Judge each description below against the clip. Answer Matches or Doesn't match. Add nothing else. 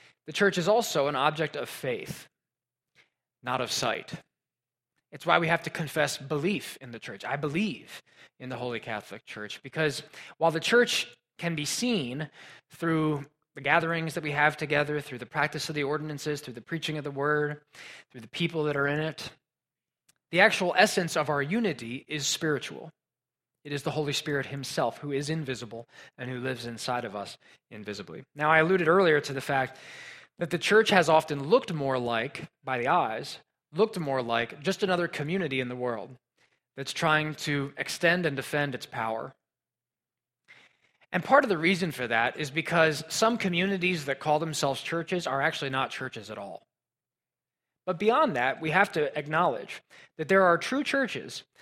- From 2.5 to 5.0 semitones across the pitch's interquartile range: Matches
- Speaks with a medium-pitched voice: Matches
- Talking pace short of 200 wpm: Matches